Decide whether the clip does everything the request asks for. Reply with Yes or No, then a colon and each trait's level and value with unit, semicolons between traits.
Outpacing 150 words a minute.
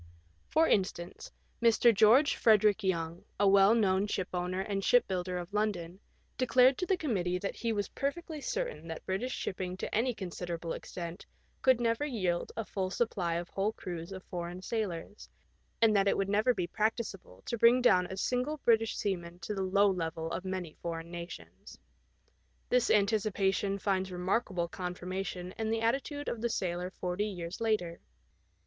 Yes: average, 165 wpm